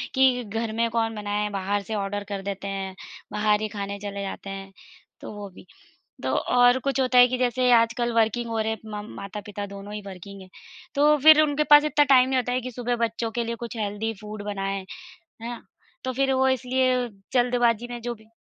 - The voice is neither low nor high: No, high, 225 Hz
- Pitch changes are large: No, average, 3.5 semitones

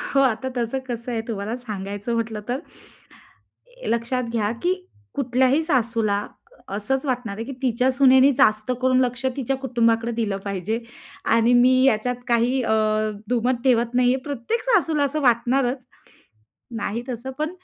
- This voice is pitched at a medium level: No, high, 245 Hz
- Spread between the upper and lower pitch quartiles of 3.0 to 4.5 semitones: No, narrow, 2.5 semitones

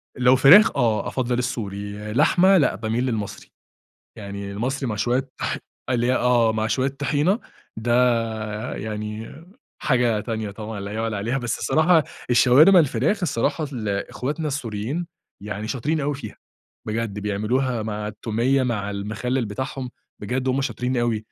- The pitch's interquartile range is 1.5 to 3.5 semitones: No, average, 3.9 semitones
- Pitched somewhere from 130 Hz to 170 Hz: No, low, 120 Hz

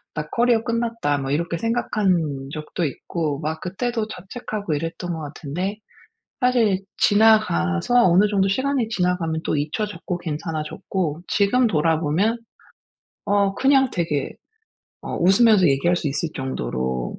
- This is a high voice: No, medium, 180 Hz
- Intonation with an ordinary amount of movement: No, wide, 6.1 semitones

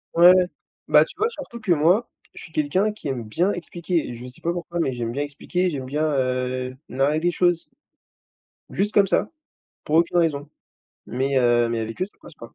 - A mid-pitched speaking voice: Yes, medium, 155 Hz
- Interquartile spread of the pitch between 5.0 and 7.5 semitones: Yes, wide, 5.6 semitones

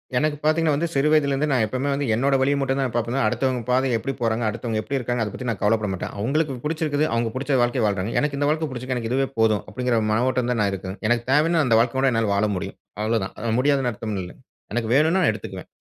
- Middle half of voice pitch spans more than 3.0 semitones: Yes, average, 3.9 semitones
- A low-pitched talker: Yes, low, 125 Hz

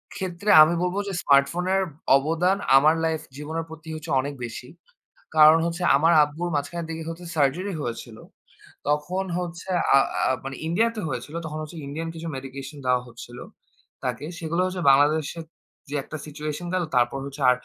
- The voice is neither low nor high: Yes, medium, 155 Hz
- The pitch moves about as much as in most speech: Yes, average, 3.5 semitones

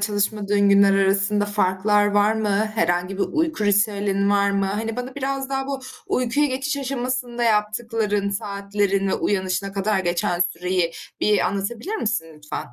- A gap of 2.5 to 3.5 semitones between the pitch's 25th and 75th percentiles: Yes, average, 2.9 semitones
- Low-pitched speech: No, high, 205 Hz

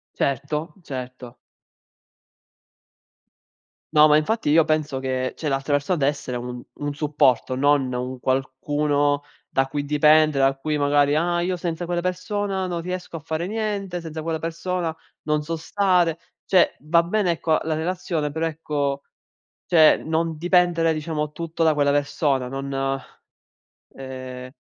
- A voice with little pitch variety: No, average, 3.2 semitones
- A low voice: No, medium, 150 Hz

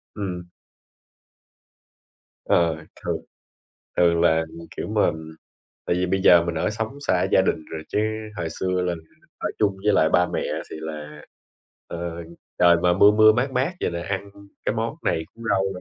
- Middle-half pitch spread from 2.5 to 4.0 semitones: Yes, average, 3.2 semitones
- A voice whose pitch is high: No, very low, 90 Hz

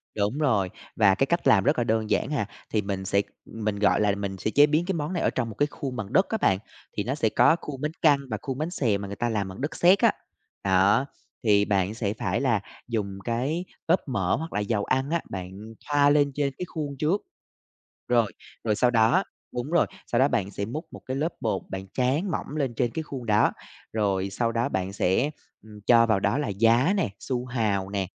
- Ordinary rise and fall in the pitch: No, wide, 6.0 semitones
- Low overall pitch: Yes, low, 115 Hz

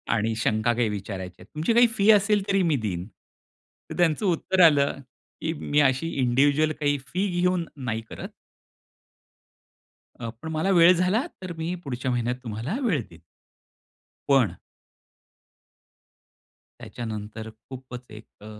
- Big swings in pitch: Yes, wide, 7.5 semitones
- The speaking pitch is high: No, medium, 140 Hz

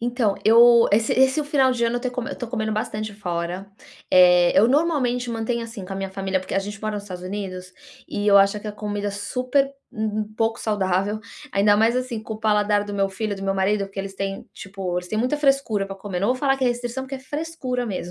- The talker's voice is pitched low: No, high, 215 Hz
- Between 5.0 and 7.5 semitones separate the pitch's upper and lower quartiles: No, average, 3.9 semitones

